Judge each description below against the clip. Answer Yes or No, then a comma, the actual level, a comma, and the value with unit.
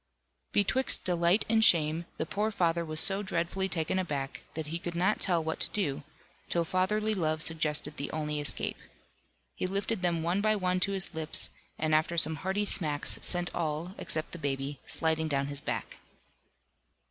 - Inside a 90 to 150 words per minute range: No, average, 175 wpm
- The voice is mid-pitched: Yes, medium, 170 Hz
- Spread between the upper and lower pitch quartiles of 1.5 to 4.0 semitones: Yes, average, 3.3 semitones